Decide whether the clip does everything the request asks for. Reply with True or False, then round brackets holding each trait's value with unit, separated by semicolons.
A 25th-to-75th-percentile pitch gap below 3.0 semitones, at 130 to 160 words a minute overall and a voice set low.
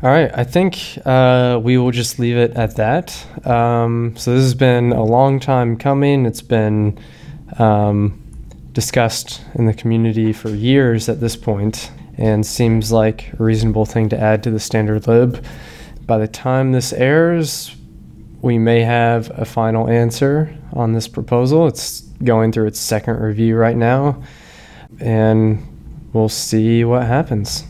True (2.6 semitones; 155 wpm; 115 Hz)